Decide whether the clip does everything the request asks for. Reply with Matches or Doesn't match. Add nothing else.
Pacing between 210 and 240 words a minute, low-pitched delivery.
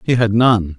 Matches